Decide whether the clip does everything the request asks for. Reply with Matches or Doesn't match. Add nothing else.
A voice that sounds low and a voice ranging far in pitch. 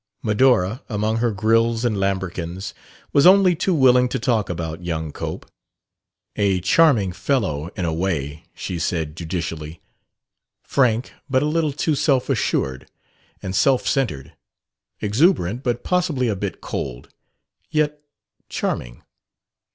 Matches